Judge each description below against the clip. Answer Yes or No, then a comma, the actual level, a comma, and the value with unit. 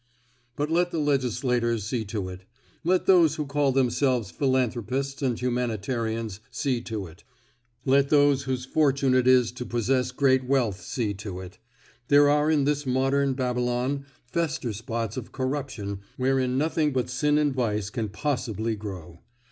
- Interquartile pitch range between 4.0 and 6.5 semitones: No, average, 3.5 semitones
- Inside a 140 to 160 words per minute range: Yes, average, 155 wpm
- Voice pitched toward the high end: No, low, 130 Hz